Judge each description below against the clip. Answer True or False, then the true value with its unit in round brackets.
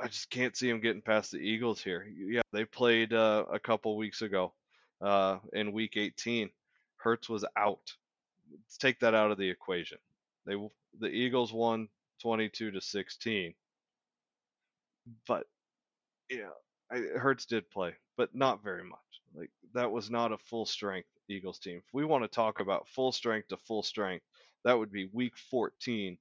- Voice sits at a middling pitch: False (110 Hz)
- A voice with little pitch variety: True (2.0 semitones)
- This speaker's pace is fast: False (170 wpm)